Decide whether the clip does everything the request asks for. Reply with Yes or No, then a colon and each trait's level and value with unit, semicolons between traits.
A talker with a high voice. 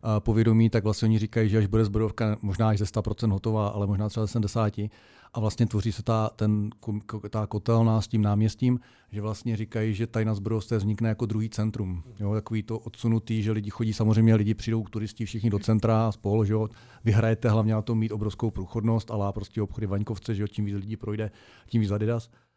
No: low, 110 Hz